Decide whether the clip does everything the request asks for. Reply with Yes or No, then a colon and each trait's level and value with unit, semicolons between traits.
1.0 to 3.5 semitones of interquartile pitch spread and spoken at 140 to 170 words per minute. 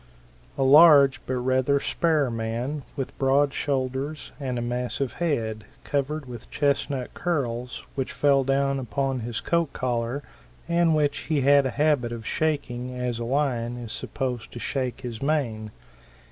Yes: average, 2.8 semitones; average, 150 wpm